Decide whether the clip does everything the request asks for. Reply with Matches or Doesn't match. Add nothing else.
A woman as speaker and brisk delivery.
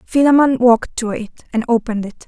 Doesn't match